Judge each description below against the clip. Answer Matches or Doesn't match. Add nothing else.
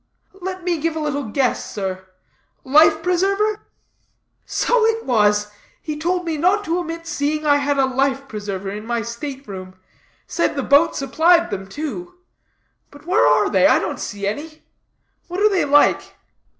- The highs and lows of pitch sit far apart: Matches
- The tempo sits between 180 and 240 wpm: Doesn't match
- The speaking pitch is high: Matches